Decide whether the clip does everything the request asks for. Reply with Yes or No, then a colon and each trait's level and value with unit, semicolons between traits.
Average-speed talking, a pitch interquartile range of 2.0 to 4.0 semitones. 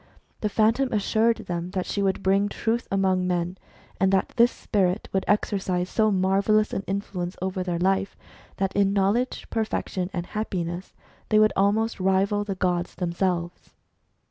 Yes: average, 150 wpm; narrow, 2.5 semitones